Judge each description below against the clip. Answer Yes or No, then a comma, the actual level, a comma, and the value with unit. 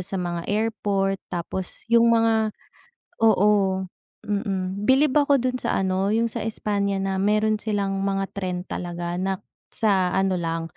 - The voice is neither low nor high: No, high, 195 Hz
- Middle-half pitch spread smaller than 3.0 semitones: Yes, narrow, 2.6 semitones